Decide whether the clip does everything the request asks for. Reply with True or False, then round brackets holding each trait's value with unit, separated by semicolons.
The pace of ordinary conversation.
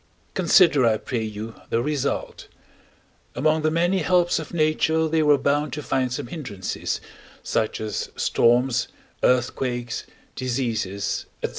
False (130 wpm)